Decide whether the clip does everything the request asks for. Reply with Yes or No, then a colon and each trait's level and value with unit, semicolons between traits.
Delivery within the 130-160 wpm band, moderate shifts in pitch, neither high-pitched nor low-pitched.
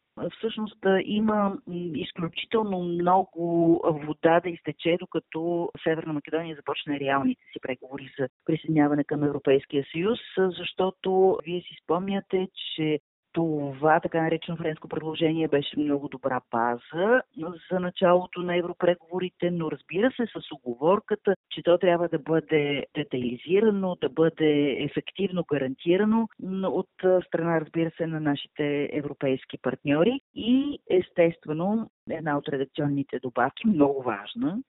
No: average, 120 wpm; average, 4.0 semitones; medium, 165 Hz